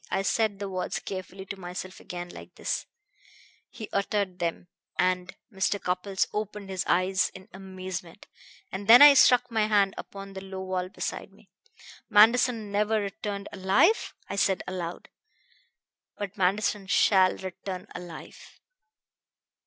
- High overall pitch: Yes, high, 195 Hz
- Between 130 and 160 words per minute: Yes, average, 140 wpm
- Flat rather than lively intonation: Yes, narrow, 1.9 semitones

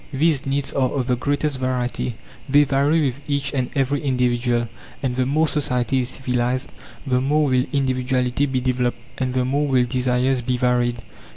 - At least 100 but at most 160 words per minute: No, average, 175 wpm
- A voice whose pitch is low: Yes, low, 130 Hz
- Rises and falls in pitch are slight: Yes, narrow, 1.9 semitones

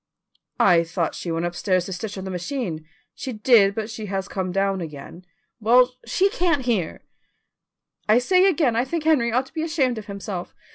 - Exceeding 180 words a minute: Yes, average, 190 wpm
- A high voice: Yes, high, 210 Hz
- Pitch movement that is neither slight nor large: No, wide, 5.9 semitones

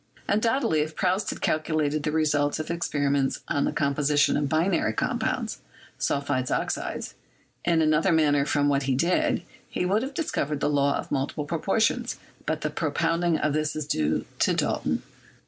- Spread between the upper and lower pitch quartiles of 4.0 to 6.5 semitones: No, average, 2.8 semitones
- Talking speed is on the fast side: No, average, 165 wpm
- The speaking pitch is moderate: Yes, medium, 155 Hz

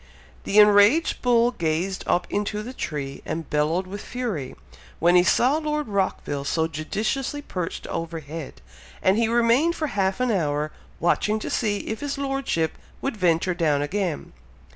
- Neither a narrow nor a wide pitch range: No, wide, 6.6 semitones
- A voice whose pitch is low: No, high, 195 Hz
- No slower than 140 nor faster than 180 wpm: Yes, average, 155 wpm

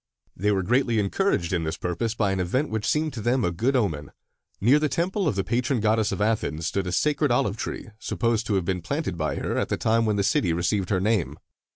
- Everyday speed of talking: No, fast, 240 wpm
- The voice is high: No, low, 105 Hz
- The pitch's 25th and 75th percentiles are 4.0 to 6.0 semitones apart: Yes, average, 5.1 semitones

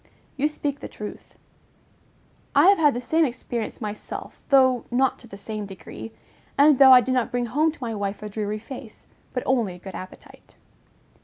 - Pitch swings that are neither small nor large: Yes, average, 4.4 semitones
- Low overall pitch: No, high, 245 Hz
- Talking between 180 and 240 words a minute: Yes, average, 185 wpm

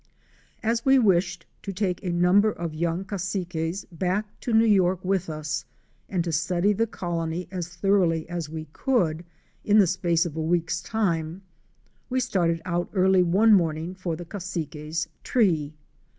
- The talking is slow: No, average, 160 wpm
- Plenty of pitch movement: No, average, 2.9 semitones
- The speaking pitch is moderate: Yes, medium, 175 Hz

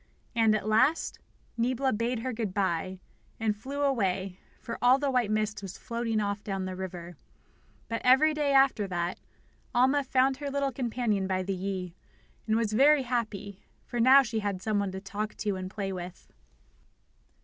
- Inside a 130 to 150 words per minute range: No, average, 180 wpm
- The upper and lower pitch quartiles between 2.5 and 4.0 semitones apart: No, average, 4.8 semitones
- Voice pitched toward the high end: Yes, high, 215 Hz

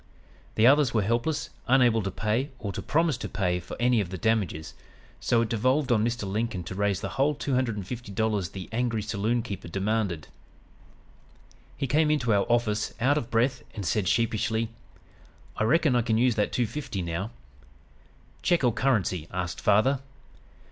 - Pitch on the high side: No, low, 115 Hz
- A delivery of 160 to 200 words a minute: Yes, average, 180 wpm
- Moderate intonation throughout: Yes, average, 3.8 semitones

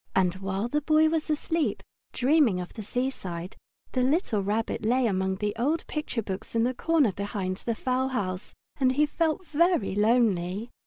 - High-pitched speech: Yes, high, 235 Hz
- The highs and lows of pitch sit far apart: Yes, wide, 7.2 semitones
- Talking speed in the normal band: Yes, average, 170 wpm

